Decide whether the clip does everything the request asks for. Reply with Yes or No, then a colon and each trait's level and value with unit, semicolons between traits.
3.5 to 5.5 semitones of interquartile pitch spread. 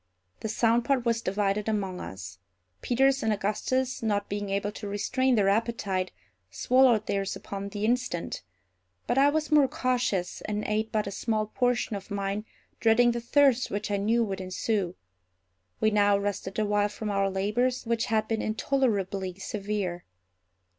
No: average, 3.0 semitones